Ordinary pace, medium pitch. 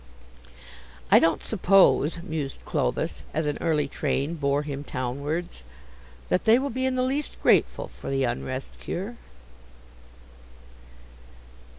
No: slow, 120 wpm; medium, 160 Hz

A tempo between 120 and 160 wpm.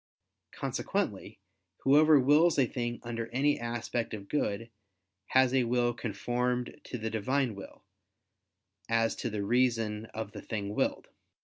Yes: slow, 135 wpm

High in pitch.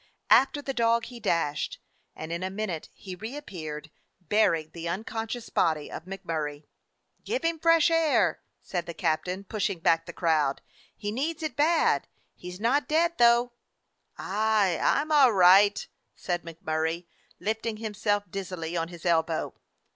Yes: high, 195 Hz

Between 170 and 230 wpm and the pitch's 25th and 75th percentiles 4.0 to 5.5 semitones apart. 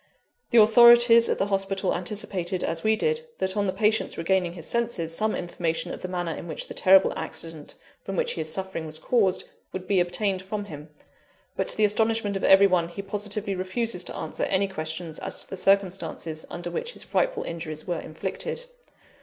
No: average, 195 wpm; average, 3.5 semitones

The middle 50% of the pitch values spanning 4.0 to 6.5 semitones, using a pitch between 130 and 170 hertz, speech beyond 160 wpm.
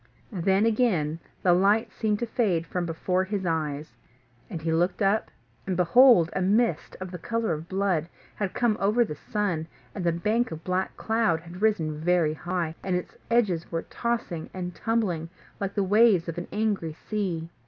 No: average, 4.3 semitones; medium, 185 Hz; average, 180 wpm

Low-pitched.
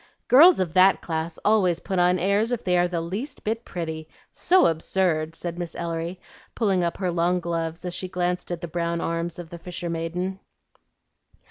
No: medium, 175 Hz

